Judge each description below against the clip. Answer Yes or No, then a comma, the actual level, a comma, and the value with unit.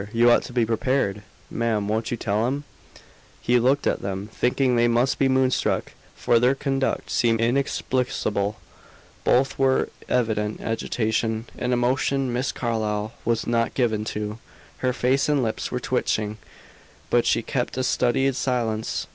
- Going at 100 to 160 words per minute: Yes, average, 155 wpm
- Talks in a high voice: No, low, 120 Hz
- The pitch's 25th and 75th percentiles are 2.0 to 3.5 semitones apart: Yes, average, 2.7 semitones